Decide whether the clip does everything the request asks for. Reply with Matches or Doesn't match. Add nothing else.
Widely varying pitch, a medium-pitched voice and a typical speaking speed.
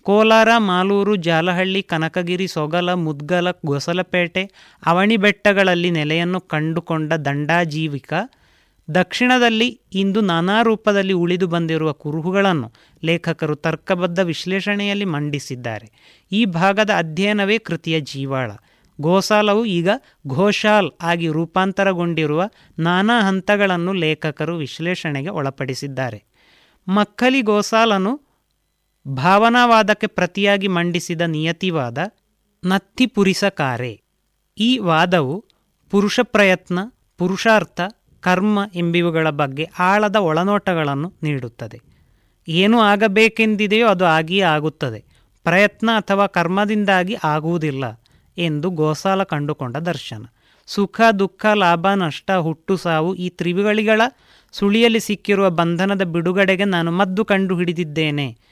Doesn't match